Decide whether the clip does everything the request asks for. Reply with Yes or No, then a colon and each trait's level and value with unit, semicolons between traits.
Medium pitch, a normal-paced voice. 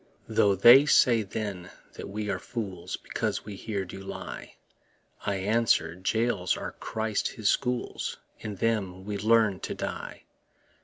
No: low, 105 Hz; average, 145 wpm